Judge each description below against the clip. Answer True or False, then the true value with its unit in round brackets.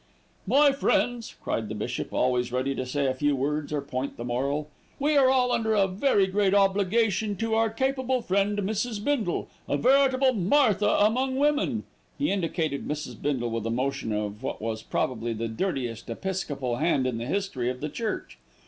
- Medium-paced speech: True (180 wpm)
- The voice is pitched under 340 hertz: True (185 Hz)